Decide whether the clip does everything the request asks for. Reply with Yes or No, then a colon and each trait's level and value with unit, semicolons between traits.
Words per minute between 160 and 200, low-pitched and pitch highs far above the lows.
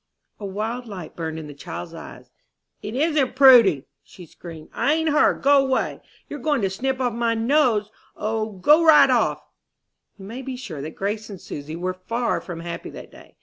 No: average, 190 wpm; high, 220 Hz; wide, 6.4 semitones